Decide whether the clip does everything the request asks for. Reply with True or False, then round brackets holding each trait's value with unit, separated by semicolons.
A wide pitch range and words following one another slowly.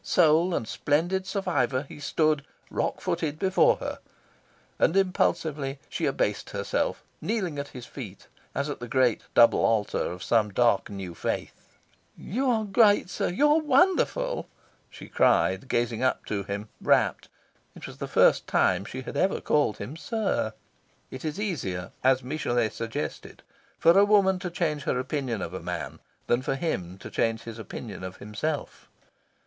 False (8.1 semitones; 165 wpm)